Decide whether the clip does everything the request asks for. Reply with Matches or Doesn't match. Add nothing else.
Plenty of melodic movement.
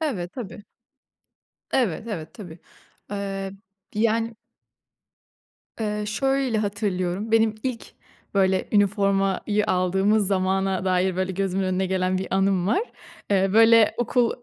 Doesn't match